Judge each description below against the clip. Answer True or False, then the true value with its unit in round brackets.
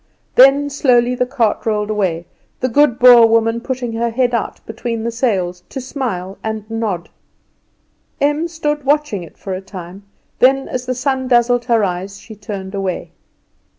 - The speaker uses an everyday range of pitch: True (4.1 semitones)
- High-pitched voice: True (235 Hz)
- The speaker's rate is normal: True (165 wpm)